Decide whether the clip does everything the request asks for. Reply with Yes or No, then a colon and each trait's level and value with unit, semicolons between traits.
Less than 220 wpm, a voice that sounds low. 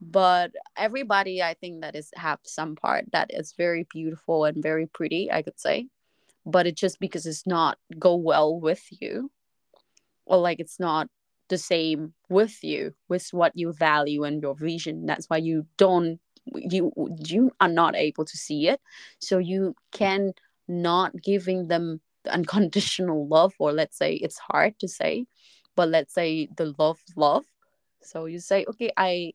No: average, 170 wpm; medium, 175 Hz